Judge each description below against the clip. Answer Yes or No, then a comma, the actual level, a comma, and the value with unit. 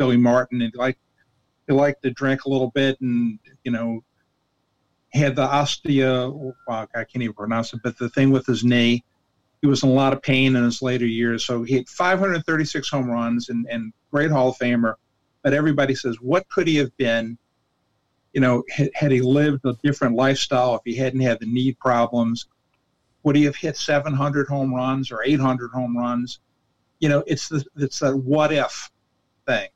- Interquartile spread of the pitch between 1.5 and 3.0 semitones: Yes, average, 2.7 semitones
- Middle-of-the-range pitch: No, low, 130 Hz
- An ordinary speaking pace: Yes, average, 195 wpm